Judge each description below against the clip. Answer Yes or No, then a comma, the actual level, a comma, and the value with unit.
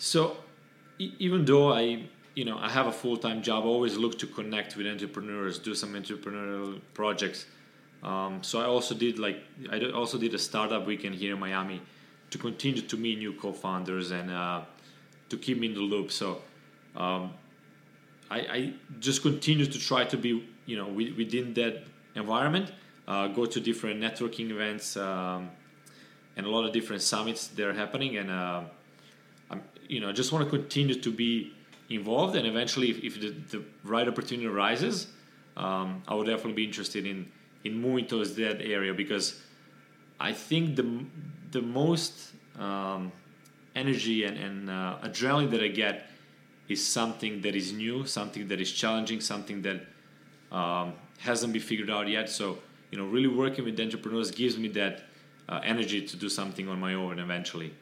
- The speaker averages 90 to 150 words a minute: No, average, 170 wpm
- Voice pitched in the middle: No, low, 110 Hz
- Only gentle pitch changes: No, average, 3.4 semitones